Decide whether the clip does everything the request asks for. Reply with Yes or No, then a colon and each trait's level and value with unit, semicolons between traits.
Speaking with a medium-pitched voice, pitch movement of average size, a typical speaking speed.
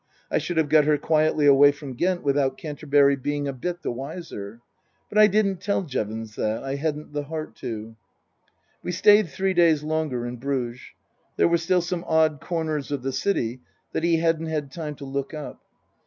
Yes: medium, 150 Hz; average, 3.5 semitones; average, 190 wpm